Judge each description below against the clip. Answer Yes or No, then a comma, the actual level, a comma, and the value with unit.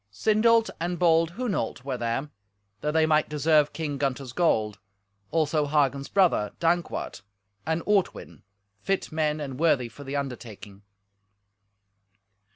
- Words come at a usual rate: No, slow, 125 wpm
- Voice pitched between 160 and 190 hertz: No, medium, 150 Hz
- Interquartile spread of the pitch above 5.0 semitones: No, average, 3.8 semitones